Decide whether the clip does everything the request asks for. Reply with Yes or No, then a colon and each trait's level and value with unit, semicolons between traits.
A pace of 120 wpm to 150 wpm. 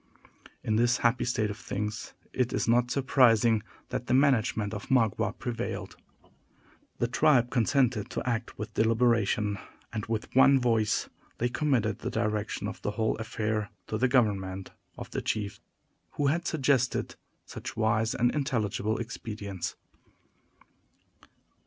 Yes: slow, 135 wpm